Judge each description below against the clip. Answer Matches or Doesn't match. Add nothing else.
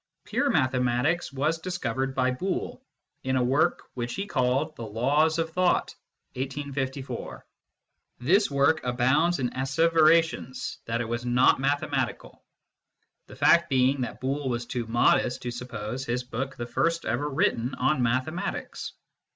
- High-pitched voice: Doesn't match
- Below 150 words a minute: Matches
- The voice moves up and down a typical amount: Matches